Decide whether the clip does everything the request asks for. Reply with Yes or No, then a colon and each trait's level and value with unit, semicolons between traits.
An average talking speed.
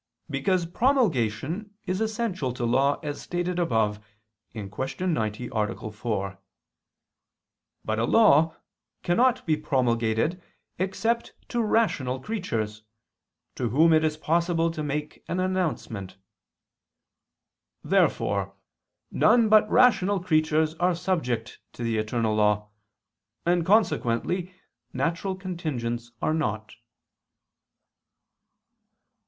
No: slow, 100 wpm